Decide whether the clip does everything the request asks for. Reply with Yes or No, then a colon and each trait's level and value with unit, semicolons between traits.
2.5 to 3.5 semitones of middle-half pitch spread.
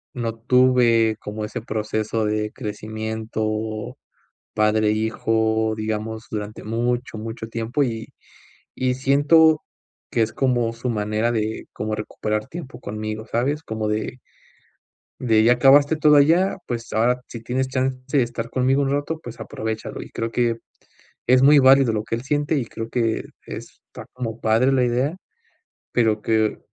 Yes: average, 2.8 semitones